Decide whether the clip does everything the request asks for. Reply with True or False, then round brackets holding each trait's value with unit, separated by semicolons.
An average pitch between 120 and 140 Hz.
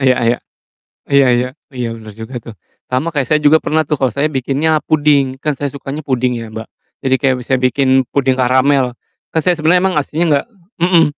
True (135 Hz)